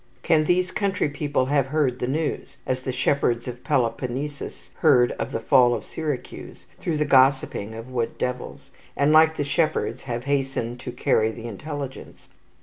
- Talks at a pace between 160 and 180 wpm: Yes, average, 165 wpm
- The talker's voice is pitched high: No, low, 135 Hz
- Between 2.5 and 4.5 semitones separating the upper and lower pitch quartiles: Yes, average, 3.4 semitones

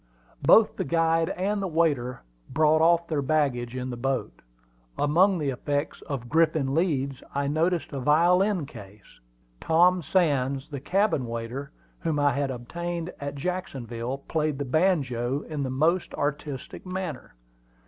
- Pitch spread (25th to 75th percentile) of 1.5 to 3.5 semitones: No, average, 4.0 semitones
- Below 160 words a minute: Yes, average, 145 wpm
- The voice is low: No, medium, 145 Hz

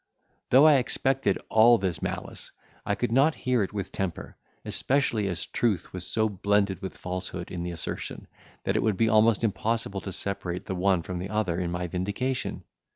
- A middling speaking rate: Yes, average, 185 wpm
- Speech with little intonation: No, average, 3.9 semitones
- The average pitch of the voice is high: No, low, 100 Hz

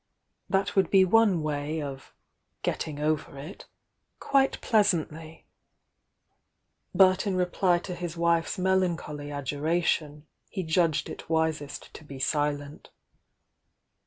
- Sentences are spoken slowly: Yes, slow, 115 wpm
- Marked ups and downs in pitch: No, average, 3.9 semitones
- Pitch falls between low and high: Yes, medium, 160 Hz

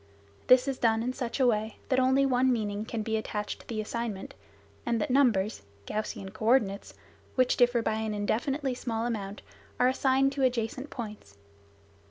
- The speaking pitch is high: Yes, high, 235 Hz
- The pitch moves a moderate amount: Yes, average, 3.1 semitones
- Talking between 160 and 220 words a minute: Yes, average, 170 wpm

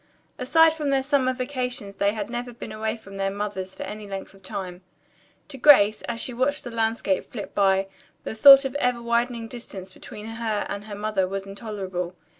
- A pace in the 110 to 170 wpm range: No, average, 200 wpm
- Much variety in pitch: No, average, 4.0 semitones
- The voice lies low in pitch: No, high, 220 Hz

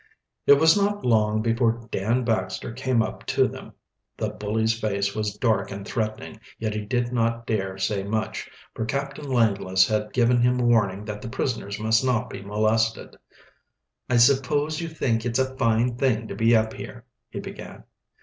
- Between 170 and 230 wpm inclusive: Yes, average, 175 wpm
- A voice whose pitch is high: No, low, 115 Hz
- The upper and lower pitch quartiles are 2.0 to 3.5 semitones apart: Yes, average, 2.7 semitones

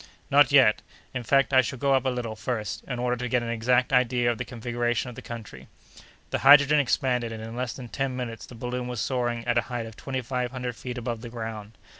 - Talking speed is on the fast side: Yes, fast, 240 wpm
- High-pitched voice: No, low, 125 Hz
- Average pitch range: No, narrow, 1.6 semitones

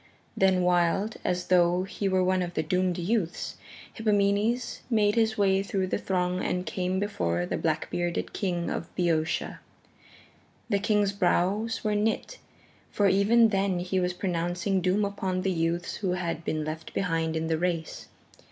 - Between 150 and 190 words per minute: Yes, average, 160 wpm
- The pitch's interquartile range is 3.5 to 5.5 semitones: No, narrow, 2.5 semitones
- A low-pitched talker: No, medium, 185 Hz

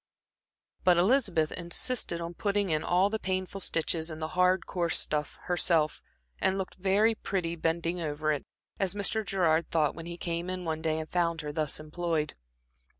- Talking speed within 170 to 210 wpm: Yes, average, 175 wpm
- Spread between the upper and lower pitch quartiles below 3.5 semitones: Yes, average, 2.8 semitones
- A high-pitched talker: No, medium, 170 Hz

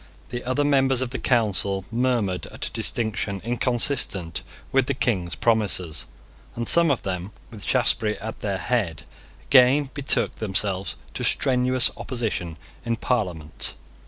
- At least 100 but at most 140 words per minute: Yes, slow, 135 wpm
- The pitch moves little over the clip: No, average, 4.7 semitones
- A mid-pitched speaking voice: No, low, 115 Hz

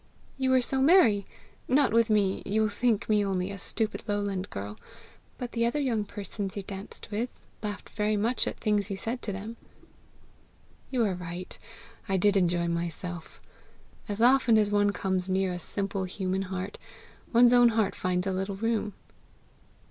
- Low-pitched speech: No, high, 205 Hz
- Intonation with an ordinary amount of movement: Yes, average, 3.2 semitones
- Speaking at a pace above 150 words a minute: Yes, average, 170 wpm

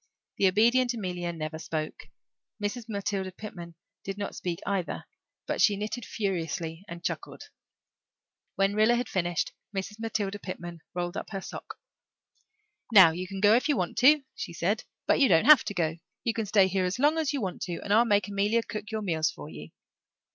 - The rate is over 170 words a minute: Yes, average, 190 wpm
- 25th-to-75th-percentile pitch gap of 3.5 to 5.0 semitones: Yes, average, 3.9 semitones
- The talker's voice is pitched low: No, high, 195 Hz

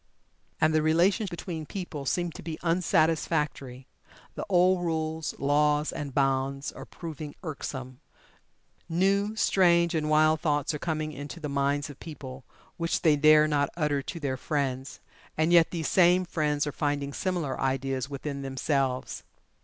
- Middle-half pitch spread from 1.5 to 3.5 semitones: Yes, average, 3.0 semitones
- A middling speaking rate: Yes, average, 150 wpm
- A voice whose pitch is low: No, medium, 155 Hz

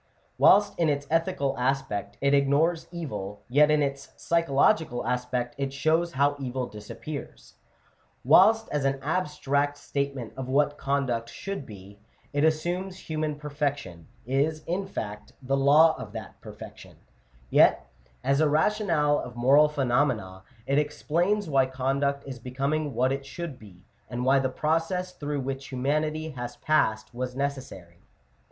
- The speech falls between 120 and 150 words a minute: Yes, average, 145 wpm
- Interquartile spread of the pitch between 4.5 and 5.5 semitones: No, average, 3.3 semitones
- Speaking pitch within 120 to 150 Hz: Yes, medium, 140 Hz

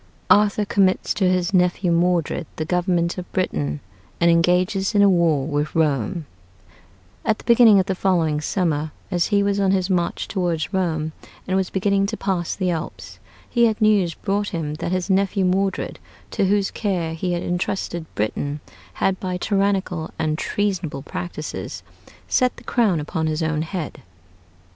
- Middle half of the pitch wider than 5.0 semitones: No, average, 3.3 semitones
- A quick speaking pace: No, average, 165 wpm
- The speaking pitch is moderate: Yes, medium, 180 Hz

